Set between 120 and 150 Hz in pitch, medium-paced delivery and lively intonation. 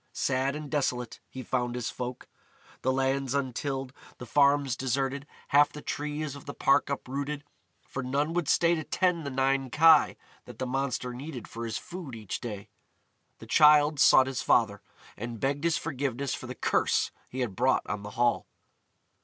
No: low, 135 Hz; average, 175 wpm; average, 2.7 semitones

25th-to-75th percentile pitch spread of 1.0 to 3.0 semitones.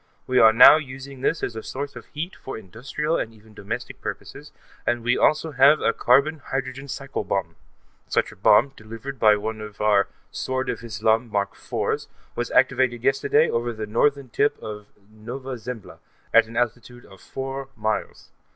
No: average, 3.7 semitones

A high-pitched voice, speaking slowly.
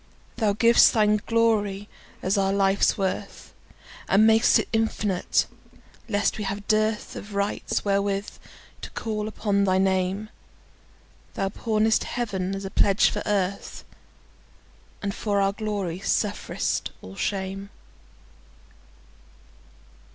Yes: high, 200 Hz; slow, 105 wpm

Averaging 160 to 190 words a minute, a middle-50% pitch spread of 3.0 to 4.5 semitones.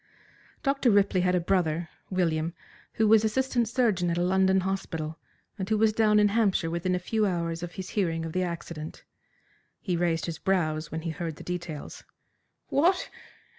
Yes: average, 175 wpm; average, 3.9 semitones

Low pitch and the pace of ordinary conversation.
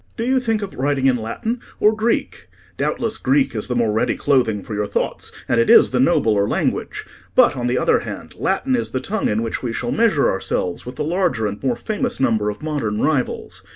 No: low, 130 Hz; fast, 220 wpm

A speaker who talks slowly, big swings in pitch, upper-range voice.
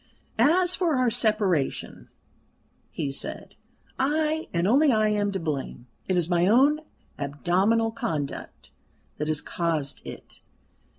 Yes: slow, 125 wpm; wide, 8.4 semitones; high, 205 Hz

